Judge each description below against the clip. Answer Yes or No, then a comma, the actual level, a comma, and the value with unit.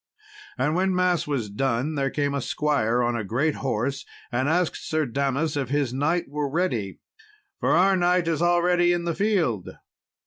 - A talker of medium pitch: Yes, medium, 145 Hz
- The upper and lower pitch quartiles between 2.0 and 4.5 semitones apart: No, average, 5.0 semitones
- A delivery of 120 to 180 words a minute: Yes, average, 175 wpm